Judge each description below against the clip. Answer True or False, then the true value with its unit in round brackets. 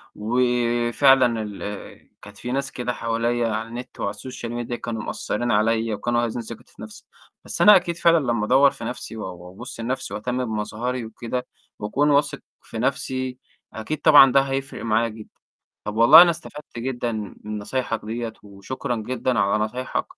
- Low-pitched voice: True (120 Hz)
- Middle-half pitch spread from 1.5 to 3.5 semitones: True (2.9 semitones)